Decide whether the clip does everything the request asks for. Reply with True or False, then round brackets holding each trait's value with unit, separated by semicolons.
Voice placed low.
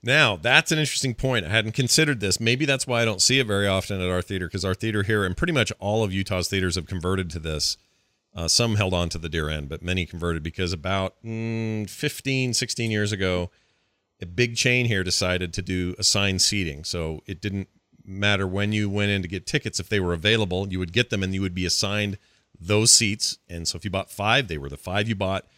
True (100 Hz)